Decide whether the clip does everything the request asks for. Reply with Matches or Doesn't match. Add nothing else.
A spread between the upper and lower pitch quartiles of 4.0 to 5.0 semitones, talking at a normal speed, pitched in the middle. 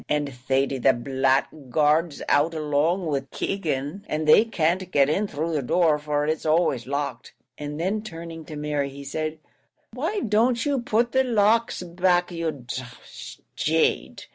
Matches